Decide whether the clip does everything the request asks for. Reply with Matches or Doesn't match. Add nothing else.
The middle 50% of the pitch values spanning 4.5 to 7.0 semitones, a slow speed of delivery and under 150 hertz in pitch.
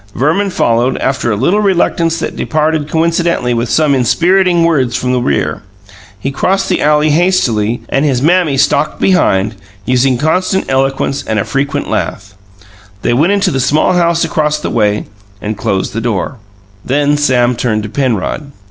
Doesn't match